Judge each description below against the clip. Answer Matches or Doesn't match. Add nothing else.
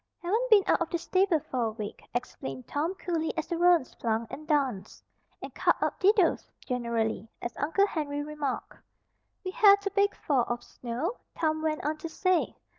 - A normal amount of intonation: Doesn't match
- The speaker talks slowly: Doesn't match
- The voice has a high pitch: Matches